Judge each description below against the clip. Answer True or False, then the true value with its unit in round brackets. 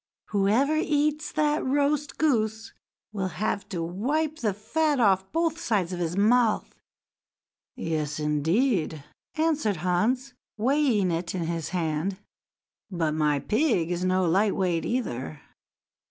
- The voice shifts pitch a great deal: True (8.1 semitones)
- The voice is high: True (205 Hz)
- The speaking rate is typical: False (125 wpm)